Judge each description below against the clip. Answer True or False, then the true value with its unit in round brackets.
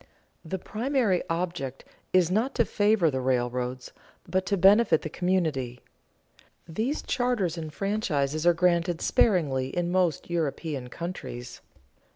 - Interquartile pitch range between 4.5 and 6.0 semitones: True (5.4 semitones)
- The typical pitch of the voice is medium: True (175 Hz)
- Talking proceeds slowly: True (125 wpm)